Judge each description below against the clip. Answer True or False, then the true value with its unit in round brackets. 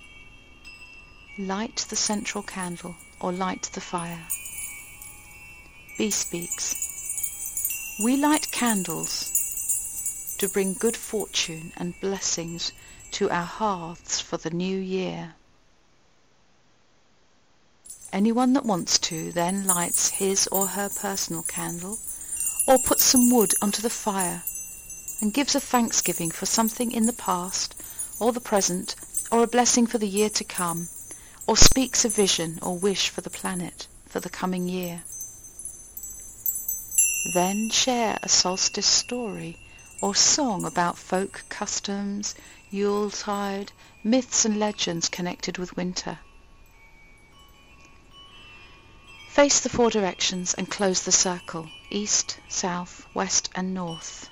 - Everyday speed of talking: False (120 wpm)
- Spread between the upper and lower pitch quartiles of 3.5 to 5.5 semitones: True (4.5 semitones)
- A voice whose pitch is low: False (185 Hz)